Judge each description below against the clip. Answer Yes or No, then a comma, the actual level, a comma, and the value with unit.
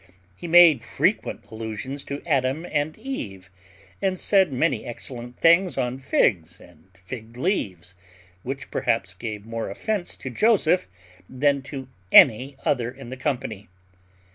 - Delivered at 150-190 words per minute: No, slow, 135 wpm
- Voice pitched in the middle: No, low, 130 Hz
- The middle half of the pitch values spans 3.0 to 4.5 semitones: No, wide, 5.6 semitones